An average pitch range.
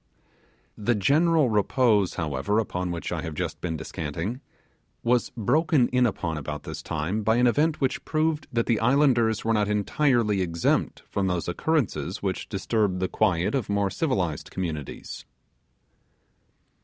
No: wide, 6.1 semitones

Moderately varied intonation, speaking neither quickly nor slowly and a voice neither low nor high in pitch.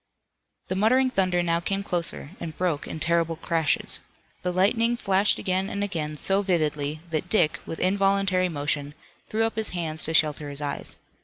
Yes: average, 3.9 semitones; average, 170 wpm; medium, 175 Hz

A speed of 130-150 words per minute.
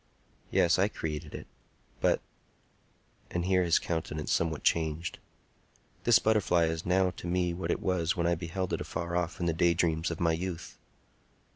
No: average, 160 wpm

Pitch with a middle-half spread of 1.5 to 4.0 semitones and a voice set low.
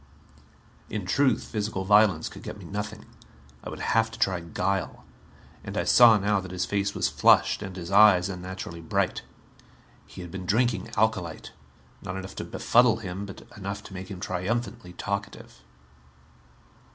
Yes: average, 2.7 semitones; low, 100 Hz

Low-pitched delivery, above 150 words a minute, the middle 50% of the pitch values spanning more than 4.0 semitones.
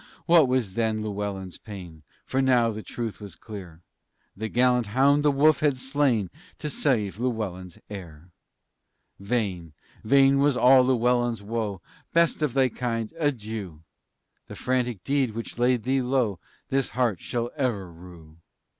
No: low, 115 Hz; average, 145 wpm; average, 4.7 semitones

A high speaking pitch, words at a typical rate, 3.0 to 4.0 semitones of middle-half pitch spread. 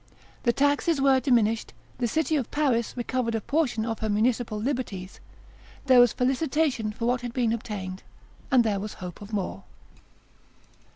Yes: high, 240 Hz; average, 160 wpm; average, 3.5 semitones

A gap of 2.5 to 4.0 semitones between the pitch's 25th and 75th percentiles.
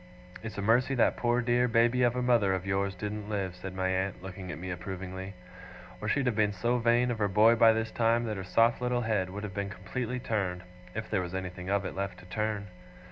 Yes: average, 3.7 semitones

